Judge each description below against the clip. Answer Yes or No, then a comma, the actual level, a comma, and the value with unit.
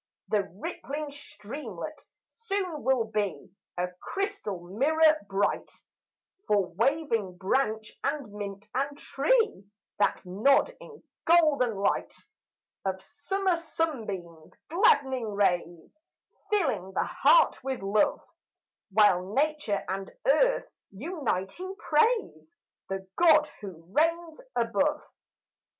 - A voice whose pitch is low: No, very high, 260 Hz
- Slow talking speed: Yes, slow, 100 wpm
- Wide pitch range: Yes, wide, 8.5 semitones